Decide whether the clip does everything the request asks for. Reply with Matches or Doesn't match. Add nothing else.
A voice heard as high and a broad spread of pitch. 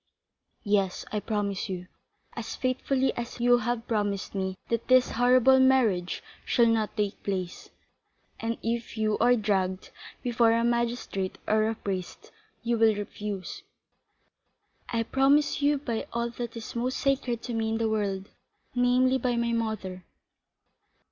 Doesn't match